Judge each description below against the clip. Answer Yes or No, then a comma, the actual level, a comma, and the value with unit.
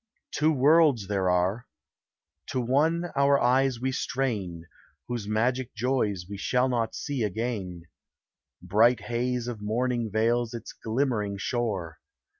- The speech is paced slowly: Yes, slow, 125 wpm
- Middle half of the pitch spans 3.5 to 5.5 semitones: Yes, average, 3.8 semitones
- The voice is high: No, low, 120 Hz